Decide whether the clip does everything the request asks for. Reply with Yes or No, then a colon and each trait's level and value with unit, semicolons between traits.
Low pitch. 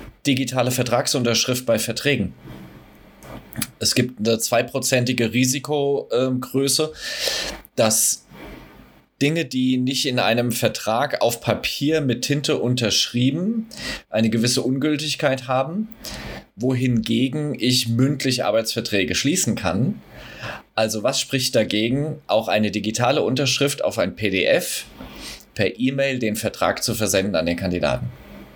Yes: low, 125 Hz